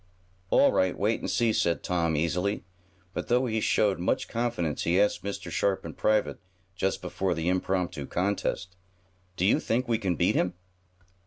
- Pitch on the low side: Yes, very low, 95 Hz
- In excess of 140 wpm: Yes, average, 170 wpm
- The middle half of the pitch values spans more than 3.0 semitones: Yes, average, 3.6 semitones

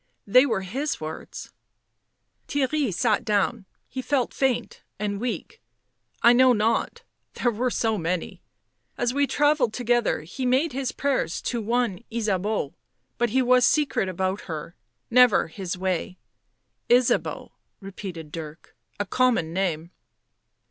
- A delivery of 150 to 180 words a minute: No, average, 140 wpm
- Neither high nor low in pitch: No, high, 225 Hz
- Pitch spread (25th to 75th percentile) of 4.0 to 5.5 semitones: Yes, average, 5.2 semitones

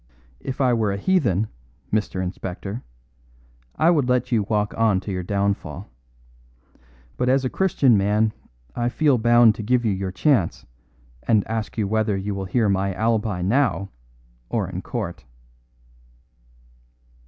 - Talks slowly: No, average, 145 wpm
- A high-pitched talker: No, low, 110 Hz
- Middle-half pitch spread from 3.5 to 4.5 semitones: Yes, average, 3.8 semitones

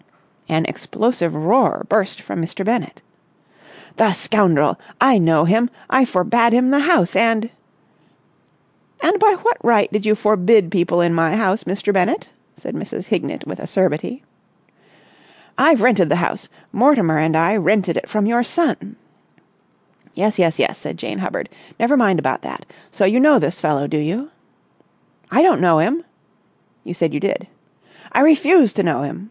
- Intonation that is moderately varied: No, wide, 6.2 semitones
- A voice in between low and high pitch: No, high, 210 Hz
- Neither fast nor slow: Yes, average, 160 wpm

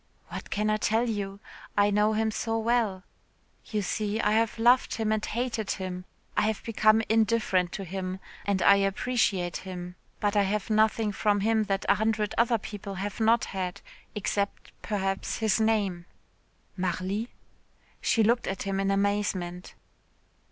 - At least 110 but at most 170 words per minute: Yes, average, 160 wpm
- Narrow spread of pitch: Yes, narrow, 2.2 semitones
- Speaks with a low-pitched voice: No, high, 210 Hz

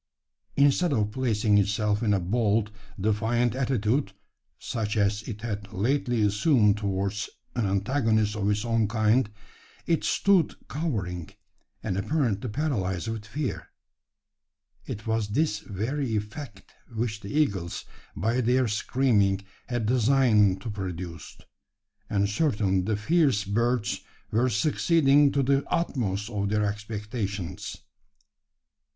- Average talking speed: No, slow, 120 wpm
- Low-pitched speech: Yes, low, 110 Hz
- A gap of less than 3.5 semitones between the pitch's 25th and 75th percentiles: No, average, 3.9 semitones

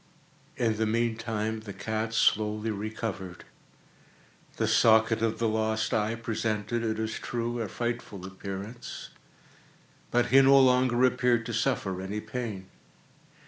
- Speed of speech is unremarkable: No, slow, 130 wpm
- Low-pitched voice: Yes, low, 110 Hz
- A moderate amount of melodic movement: No, narrow, 1.7 semitones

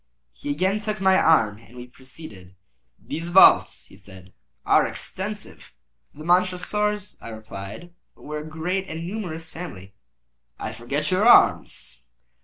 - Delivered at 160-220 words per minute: No, slow, 135 wpm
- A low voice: No, medium, 155 Hz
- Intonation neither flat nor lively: No, wide, 9.0 semitones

